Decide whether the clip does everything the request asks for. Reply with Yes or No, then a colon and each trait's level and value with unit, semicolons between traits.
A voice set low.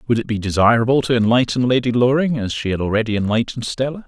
Yes: low, 120 Hz